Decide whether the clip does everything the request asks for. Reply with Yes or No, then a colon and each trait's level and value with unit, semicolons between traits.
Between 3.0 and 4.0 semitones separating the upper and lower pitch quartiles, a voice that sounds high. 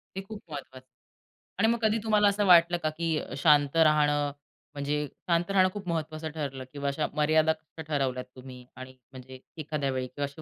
No: average, 3.5 semitones; medium, 150 Hz